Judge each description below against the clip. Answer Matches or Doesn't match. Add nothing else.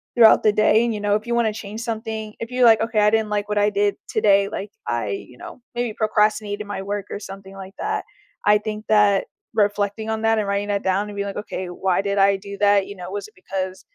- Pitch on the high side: Matches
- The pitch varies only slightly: Matches